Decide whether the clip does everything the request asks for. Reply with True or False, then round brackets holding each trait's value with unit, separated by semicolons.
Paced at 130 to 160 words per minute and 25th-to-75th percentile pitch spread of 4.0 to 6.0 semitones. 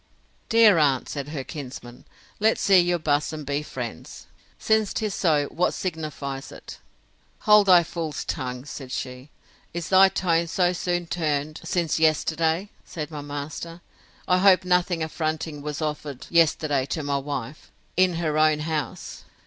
False (150 wpm; 3.4 semitones)